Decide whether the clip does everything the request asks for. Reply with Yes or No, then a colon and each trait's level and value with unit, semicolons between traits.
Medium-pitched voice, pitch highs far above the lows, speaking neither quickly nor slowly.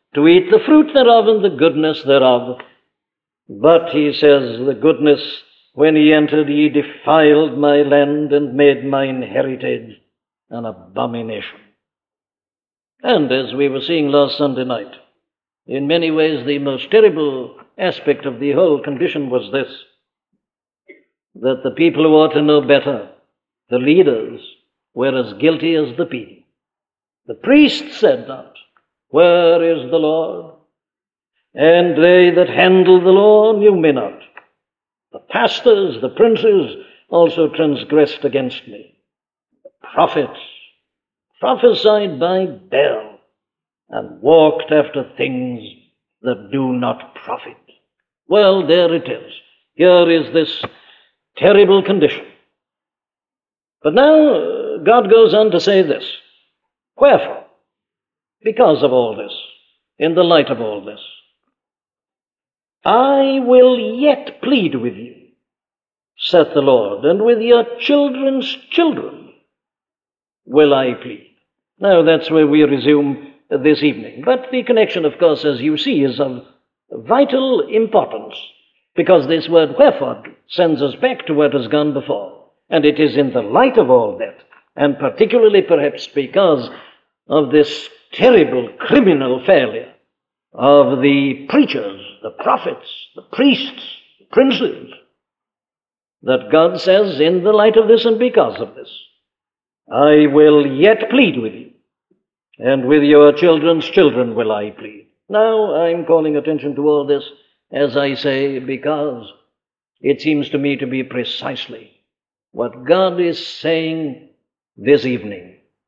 No: medium, 155 Hz; wide, 7.3 semitones; slow, 130 wpm